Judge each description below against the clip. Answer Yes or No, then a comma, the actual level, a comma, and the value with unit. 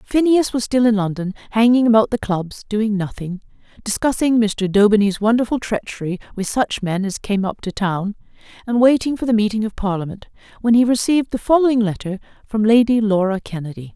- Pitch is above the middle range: Yes, high, 215 Hz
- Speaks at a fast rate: No, average, 175 wpm